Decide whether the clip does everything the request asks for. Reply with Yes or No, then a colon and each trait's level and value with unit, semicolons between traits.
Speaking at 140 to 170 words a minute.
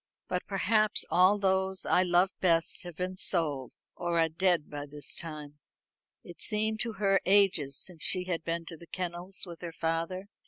No: average, 180 wpm